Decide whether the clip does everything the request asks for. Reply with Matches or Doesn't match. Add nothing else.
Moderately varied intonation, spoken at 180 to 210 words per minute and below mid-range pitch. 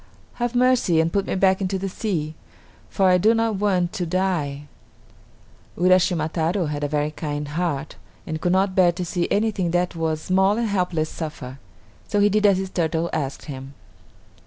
Doesn't match